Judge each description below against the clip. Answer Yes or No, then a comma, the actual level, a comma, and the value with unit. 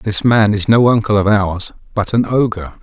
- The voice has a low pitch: Yes, low, 105 Hz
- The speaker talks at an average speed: No, fast, 210 wpm